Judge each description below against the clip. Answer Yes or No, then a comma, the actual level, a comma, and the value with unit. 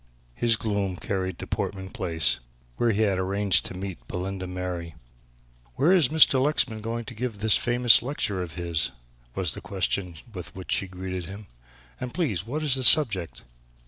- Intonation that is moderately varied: Yes, average, 4.6 semitones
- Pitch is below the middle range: Yes, low, 100 Hz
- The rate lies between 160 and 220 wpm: Yes, average, 175 wpm